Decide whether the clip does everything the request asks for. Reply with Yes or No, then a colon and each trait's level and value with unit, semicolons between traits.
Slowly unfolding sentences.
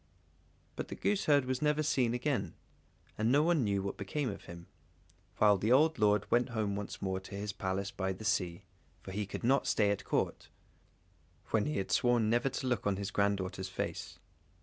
No: average, 195 wpm